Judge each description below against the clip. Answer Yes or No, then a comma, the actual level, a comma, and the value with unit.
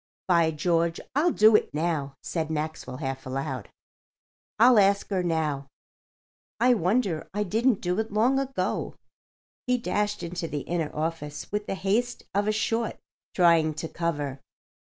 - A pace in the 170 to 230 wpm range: No, average, 150 wpm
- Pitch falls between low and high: Yes, medium, 175 Hz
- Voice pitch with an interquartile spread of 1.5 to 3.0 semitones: No, average, 5.2 semitones